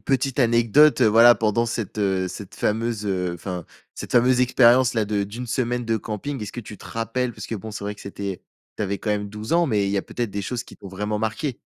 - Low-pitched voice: Yes, low, 110 Hz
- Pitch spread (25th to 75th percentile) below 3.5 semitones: Yes, average, 3.0 semitones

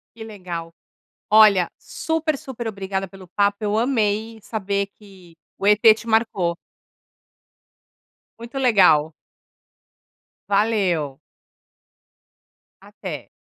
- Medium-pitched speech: No, high, 205 Hz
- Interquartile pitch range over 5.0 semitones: No, average, 3.2 semitones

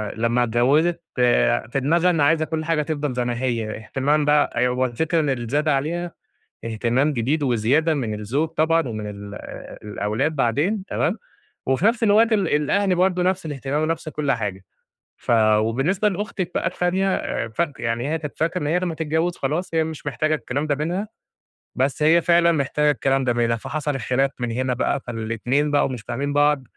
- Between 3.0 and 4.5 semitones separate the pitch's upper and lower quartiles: No, average, 4.9 semitones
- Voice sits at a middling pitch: Yes, medium, 145 Hz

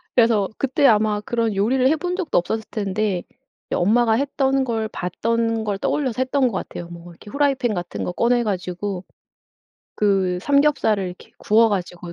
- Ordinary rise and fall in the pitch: Yes, average, 4.8 semitones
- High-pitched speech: Yes, high, 220 Hz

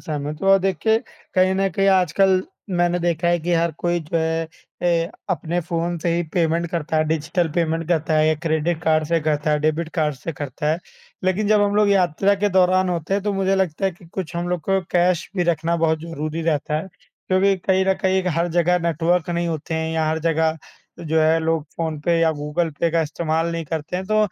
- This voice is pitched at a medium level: Yes, medium, 170 Hz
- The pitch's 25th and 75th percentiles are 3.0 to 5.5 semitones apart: No, narrow, 2.5 semitones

